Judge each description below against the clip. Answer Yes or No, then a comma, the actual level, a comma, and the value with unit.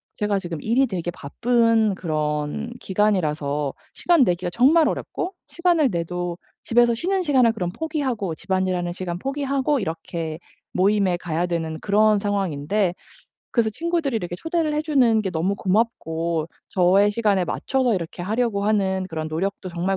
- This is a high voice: Yes, high, 200 Hz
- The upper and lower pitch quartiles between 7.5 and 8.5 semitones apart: No, wide, 5.5 semitones